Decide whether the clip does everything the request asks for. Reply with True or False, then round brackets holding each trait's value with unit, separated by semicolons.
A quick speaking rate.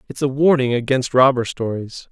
False (170 wpm)